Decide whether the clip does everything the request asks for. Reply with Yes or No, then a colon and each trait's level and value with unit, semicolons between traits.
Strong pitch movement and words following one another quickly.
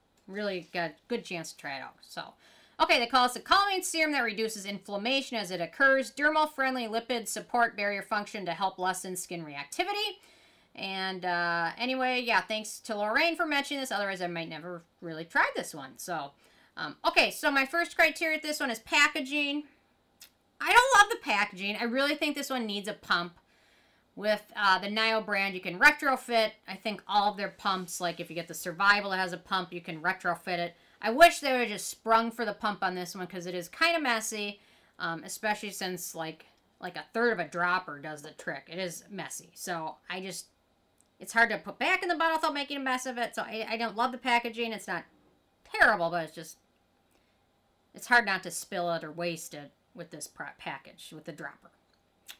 Yes: wide, 6.3 semitones; fast, 210 wpm